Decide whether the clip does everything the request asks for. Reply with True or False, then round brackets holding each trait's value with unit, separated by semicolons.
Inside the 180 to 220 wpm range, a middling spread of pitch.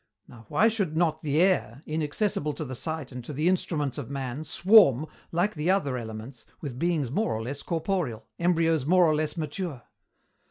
True (185 wpm; 4.4 semitones)